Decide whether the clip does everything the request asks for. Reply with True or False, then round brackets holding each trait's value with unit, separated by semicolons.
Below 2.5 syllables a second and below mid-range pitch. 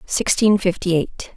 False (2.3 syllables/s; 185 Hz)